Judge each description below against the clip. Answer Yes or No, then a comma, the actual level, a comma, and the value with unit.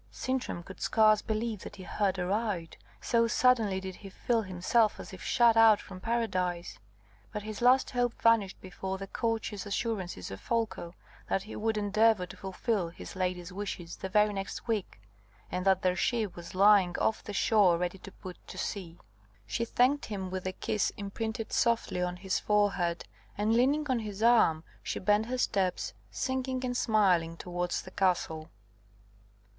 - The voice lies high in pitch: Yes, high, 205 Hz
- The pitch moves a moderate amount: Yes, average, 3.6 semitones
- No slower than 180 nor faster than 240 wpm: No, average, 170 wpm